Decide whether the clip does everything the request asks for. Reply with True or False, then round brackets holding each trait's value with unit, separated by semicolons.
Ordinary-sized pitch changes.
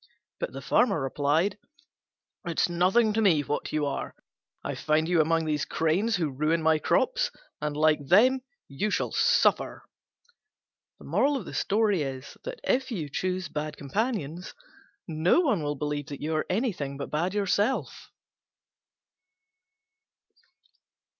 False (5.7 semitones)